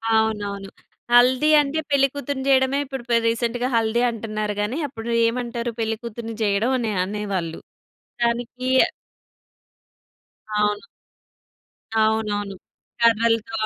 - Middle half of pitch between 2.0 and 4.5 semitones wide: Yes, average, 2.7 semitones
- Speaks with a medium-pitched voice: No, high, 230 Hz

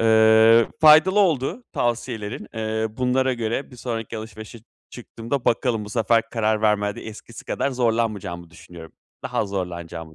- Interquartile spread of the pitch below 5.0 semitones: Yes, narrow, 2.6 semitones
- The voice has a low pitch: Yes, low, 115 Hz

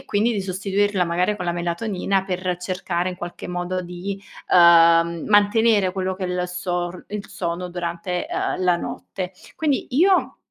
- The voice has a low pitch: No, medium, 185 Hz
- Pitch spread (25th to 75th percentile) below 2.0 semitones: No, narrow, 2.3 semitones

